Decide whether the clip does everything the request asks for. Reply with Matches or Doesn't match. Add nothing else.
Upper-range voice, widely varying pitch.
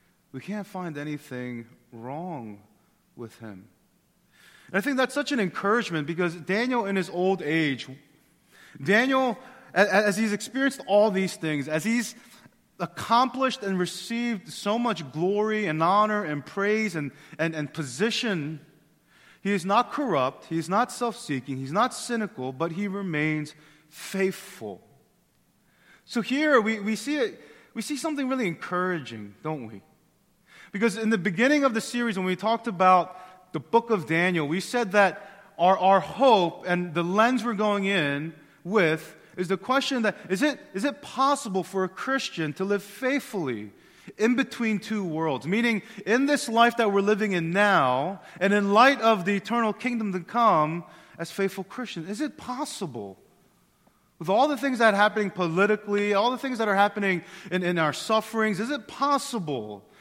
Matches